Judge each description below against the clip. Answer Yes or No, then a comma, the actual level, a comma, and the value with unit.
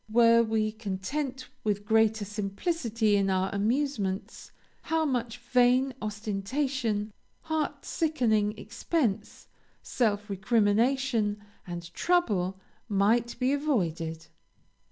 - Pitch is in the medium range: No, high, 220 Hz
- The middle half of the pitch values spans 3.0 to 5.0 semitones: Yes, average, 4.2 semitones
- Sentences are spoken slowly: Yes, slow, 95 wpm